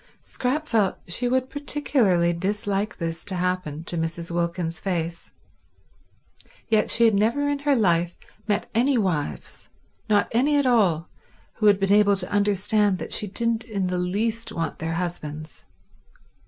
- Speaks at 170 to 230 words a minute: No, average, 155 wpm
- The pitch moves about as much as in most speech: Yes, average, 5.0 semitones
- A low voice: No, high, 200 Hz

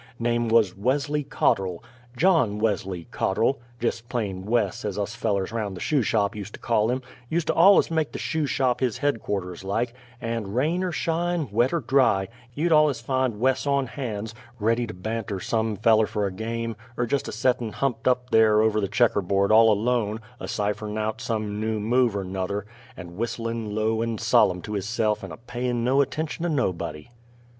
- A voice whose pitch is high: No, low, 115 Hz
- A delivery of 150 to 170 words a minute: No, average, 190 wpm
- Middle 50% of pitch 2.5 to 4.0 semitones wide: Yes, average, 3.5 semitones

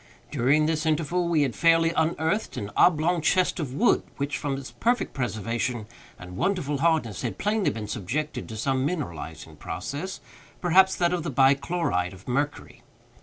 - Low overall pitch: No, medium, 150 Hz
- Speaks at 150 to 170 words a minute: Yes, average, 160 wpm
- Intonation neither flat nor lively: No, wide, 6.0 semitones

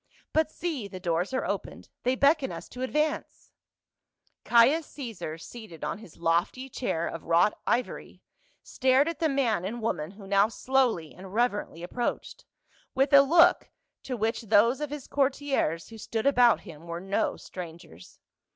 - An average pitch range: No, wide, 6.9 semitones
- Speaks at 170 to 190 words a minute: No, average, 160 wpm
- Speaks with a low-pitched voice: No, high, 230 Hz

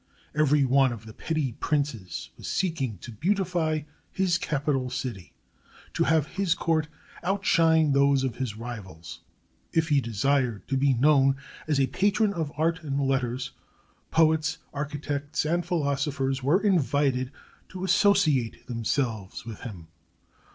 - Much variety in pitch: No, average, 4.1 semitones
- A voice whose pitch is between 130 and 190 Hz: Yes, medium, 140 Hz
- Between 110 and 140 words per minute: Yes, slow, 135 wpm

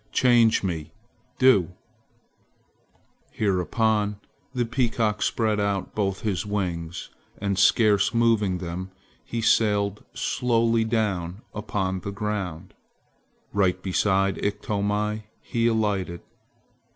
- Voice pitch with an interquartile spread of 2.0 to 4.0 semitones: Yes, average, 2.7 semitones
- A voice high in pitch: No, low, 105 Hz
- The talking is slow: Yes, slow, 95 wpm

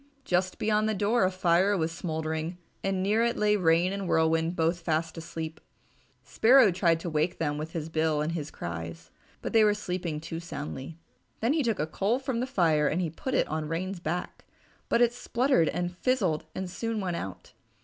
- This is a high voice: No, medium, 175 Hz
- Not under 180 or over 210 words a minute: Yes, average, 195 wpm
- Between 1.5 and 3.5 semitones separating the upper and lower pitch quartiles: No, average, 4.5 semitones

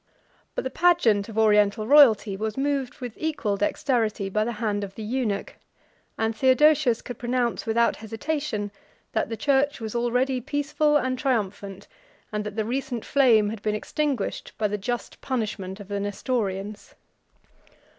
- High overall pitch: Yes, high, 225 Hz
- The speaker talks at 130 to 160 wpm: Yes, average, 155 wpm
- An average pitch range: Yes, average, 4.0 semitones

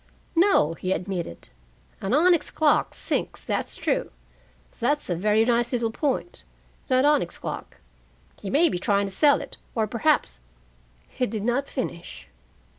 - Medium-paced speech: Yes, average, 150 wpm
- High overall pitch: Yes, high, 230 Hz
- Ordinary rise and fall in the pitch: No, wide, 7.2 semitones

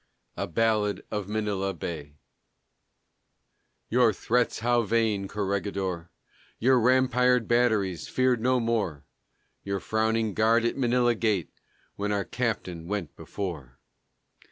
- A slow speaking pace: Yes, slow, 110 wpm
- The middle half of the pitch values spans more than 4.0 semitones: No, average, 3.4 semitones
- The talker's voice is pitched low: Yes, low, 110 Hz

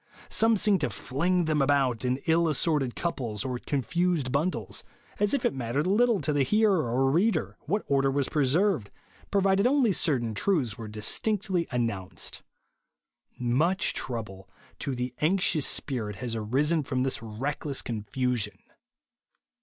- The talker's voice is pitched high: No, medium, 140 Hz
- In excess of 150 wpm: No, average, 145 wpm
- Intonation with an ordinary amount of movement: No, wide, 6.8 semitones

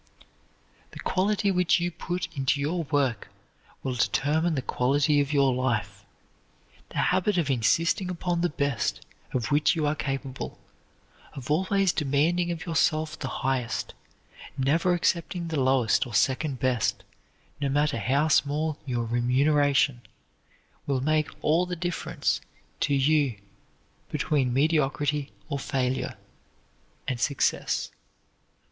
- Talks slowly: Yes, slow, 125 wpm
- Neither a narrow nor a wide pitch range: Yes, average, 3.8 semitones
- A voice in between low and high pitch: Yes, medium, 145 Hz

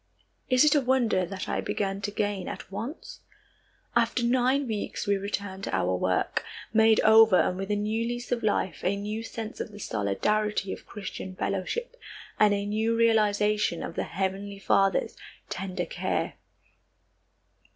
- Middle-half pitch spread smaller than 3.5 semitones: Yes, average, 2.8 semitones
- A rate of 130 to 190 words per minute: Yes, average, 160 wpm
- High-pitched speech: Yes, high, 210 Hz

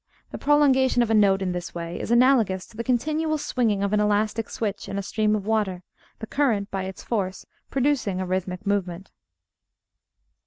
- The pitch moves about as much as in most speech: Yes, average, 4.2 semitones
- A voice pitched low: No, high, 210 Hz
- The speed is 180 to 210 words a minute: Yes, average, 185 wpm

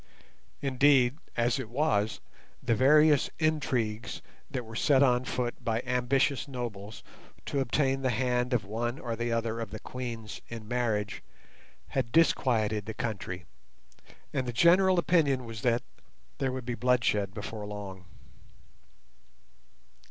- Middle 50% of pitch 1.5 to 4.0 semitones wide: Yes, average, 3.1 semitones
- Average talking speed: No, slow, 130 wpm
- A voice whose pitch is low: Yes, low, 120 Hz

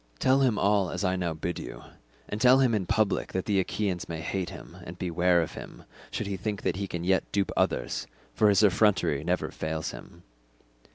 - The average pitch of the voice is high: No, very low, 95 Hz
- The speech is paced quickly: Yes, fast, 210 wpm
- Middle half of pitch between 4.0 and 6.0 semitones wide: No, average, 3.0 semitones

